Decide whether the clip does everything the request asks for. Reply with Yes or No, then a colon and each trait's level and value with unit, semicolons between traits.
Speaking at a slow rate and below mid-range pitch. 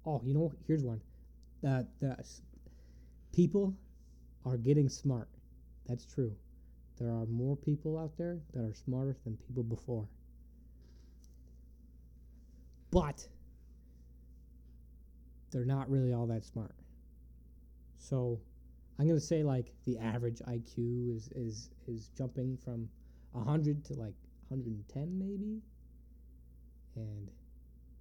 Yes: slow, 115 wpm; low, 110 Hz